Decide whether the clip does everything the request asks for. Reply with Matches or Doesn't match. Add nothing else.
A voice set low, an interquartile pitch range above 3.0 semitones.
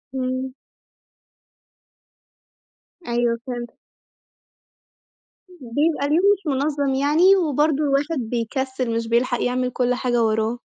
Doesn't match